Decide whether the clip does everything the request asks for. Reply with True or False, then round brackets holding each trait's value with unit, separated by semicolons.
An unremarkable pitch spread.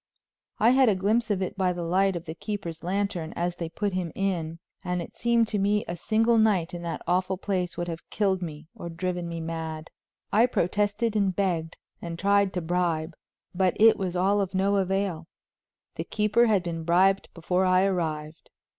True (3.0 semitones)